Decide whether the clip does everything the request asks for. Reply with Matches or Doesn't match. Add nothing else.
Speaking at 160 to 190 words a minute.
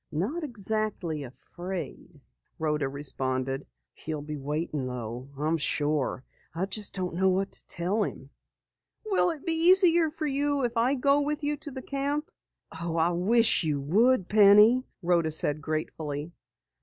Doesn't match